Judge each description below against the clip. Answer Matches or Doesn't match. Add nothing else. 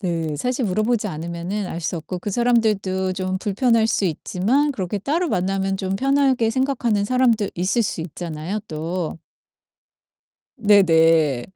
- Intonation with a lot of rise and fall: Doesn't match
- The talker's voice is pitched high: Matches